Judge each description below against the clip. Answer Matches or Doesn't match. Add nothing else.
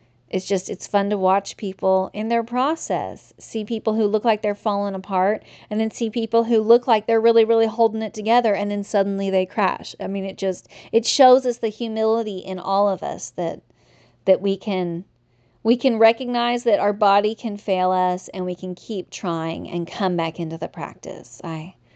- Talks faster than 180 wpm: Matches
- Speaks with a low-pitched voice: Doesn't match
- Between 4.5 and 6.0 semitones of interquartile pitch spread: Doesn't match